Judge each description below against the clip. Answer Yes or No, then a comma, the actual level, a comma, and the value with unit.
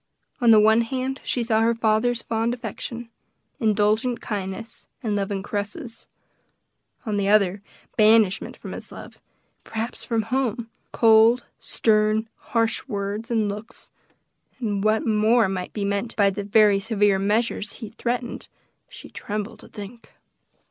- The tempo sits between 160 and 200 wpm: No, slow, 135 wpm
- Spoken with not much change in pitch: Yes, narrow, 2.1 semitones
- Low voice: No, high, 220 Hz